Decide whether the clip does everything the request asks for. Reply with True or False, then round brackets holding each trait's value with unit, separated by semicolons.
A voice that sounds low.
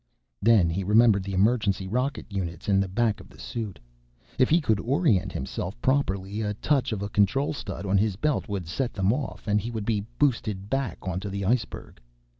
True (105 Hz)